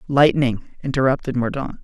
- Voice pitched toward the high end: No, low, 130 Hz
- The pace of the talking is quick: No, slow, 100 wpm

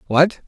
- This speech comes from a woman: No, male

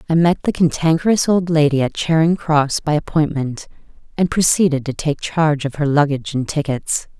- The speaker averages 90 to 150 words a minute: No, average, 175 wpm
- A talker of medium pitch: Yes, medium, 150 Hz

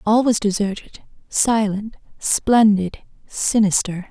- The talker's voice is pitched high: Yes, high, 210 Hz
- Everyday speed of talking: No, slow, 90 wpm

